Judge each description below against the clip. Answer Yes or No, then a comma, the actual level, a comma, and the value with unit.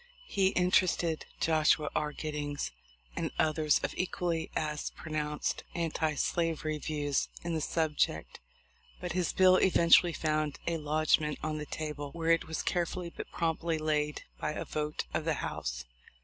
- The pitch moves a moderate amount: No, narrow, 1.9 semitones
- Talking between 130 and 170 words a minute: Yes, average, 150 wpm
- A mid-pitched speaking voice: Yes, medium, 155 Hz